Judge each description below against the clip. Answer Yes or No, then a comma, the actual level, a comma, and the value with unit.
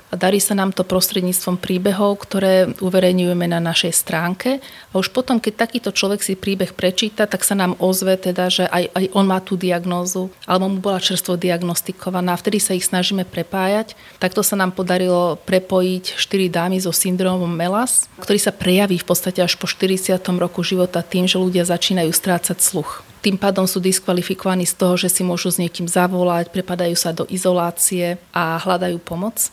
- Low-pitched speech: No, medium, 185 Hz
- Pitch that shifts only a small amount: Yes, narrow, 1.3 semitones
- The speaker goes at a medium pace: No, fast, 180 wpm